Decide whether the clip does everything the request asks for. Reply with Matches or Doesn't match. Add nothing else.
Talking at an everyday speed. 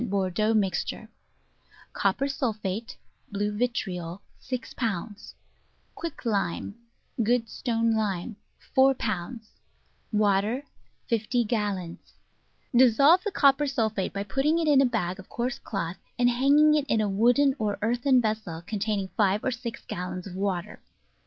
Doesn't match